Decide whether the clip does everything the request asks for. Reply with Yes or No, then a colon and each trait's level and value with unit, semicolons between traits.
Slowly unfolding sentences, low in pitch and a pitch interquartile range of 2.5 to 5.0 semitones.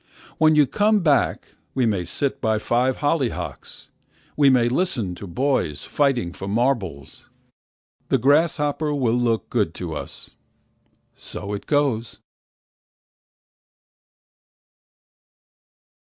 No: slow, 95 wpm; low, 125 Hz; wide, 5.6 semitones